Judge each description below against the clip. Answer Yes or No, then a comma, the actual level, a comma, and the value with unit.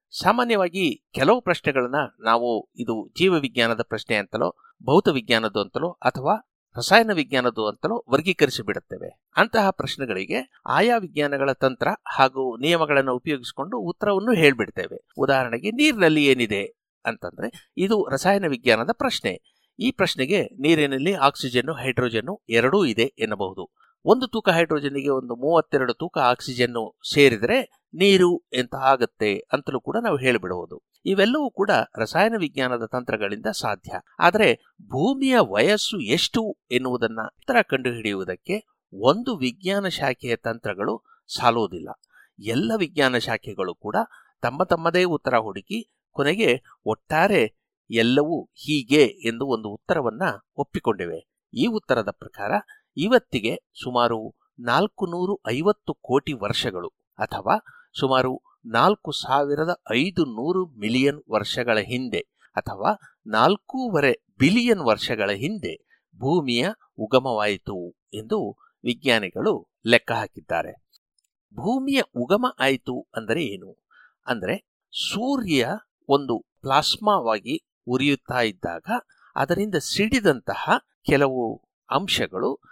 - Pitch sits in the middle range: Yes, medium, 150 Hz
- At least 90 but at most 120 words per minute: Yes, average, 100 wpm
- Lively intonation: Yes, wide, 8.6 semitones